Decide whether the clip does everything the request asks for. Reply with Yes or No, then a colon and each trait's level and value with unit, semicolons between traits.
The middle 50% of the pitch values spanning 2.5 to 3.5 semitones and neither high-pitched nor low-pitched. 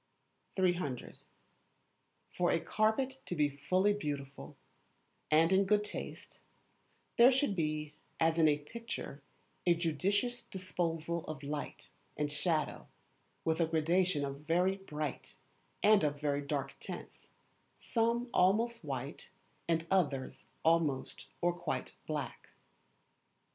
No: average, 4.4 semitones; medium, 165 Hz